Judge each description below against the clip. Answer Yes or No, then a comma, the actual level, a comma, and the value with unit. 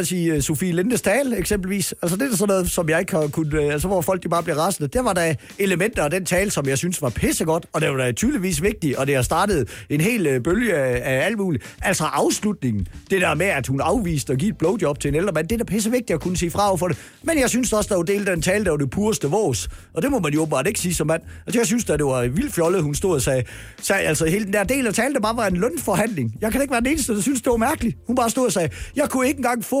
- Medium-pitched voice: Yes, medium, 180 Hz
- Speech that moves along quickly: Yes, fast, 300 wpm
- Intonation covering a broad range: Yes, wide, 6.0 semitones